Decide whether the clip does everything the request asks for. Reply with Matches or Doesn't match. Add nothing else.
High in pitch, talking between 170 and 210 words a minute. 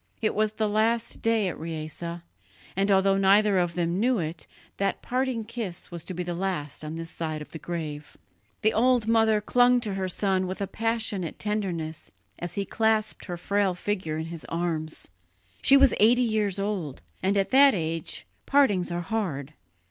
Matches